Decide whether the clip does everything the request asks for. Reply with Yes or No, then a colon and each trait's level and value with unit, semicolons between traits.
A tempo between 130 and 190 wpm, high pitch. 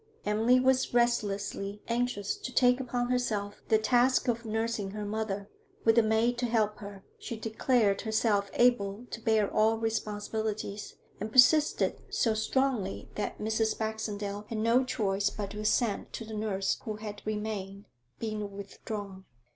Yes: average, 150 wpm; high, 220 Hz